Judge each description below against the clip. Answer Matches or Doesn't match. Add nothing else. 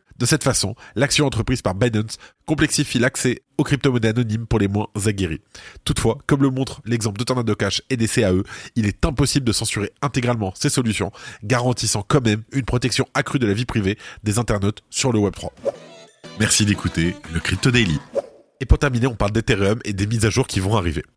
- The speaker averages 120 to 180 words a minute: Doesn't match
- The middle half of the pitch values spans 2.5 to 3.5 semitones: Doesn't match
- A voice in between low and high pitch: Doesn't match